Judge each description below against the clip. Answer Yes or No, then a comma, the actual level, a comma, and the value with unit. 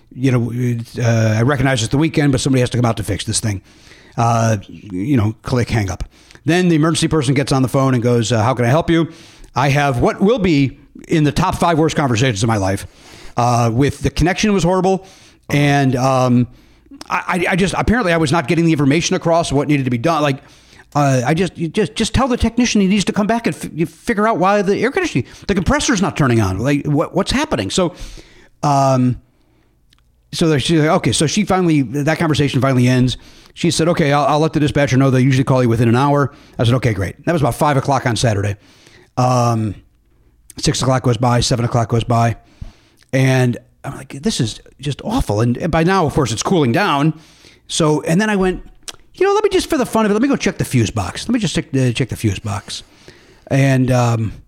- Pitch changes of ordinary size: No, wide, 5.7 semitones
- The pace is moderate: No, fast, 230 wpm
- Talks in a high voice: No, medium, 140 Hz